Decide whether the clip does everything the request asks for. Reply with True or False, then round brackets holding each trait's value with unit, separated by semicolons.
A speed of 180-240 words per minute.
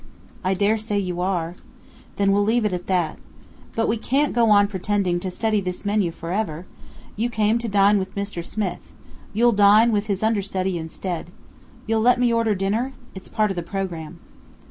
True (190 wpm)